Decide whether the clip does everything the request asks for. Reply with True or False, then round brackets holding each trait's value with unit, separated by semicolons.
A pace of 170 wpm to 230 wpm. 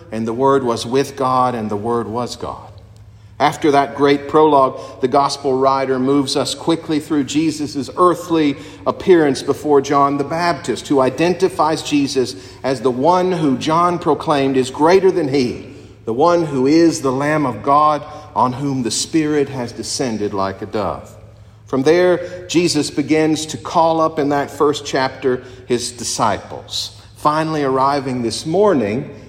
False (155 wpm)